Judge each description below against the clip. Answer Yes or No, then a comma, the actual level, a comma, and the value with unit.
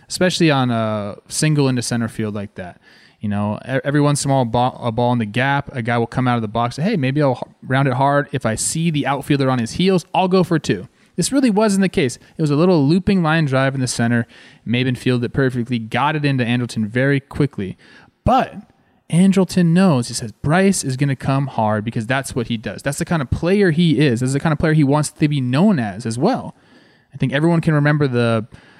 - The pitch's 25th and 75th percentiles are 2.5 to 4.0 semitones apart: No, average, 4.7 semitones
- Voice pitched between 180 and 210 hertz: No, low, 135 Hz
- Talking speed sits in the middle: No, fast, 245 wpm